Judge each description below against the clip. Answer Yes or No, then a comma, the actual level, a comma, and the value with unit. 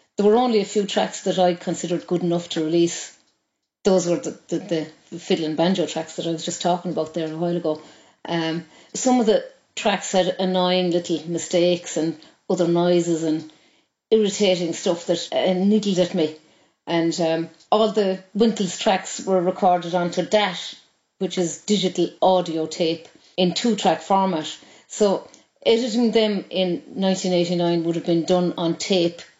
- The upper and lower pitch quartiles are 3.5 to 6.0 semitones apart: No, narrow, 2.4 semitones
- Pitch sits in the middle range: Yes, medium, 175 Hz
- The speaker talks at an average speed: Yes, average, 165 wpm